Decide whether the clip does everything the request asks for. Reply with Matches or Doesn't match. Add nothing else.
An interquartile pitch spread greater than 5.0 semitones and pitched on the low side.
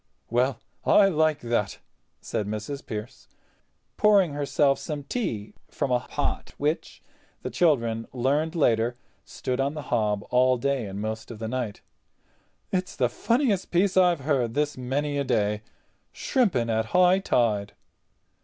Matches